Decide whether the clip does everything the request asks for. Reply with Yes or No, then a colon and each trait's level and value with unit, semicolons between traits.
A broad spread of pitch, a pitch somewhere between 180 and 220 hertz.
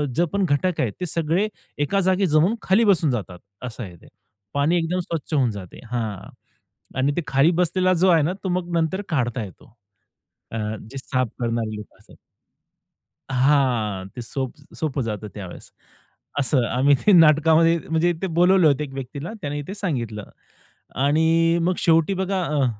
No: wide, 5.8 semitones; medium, 150 Hz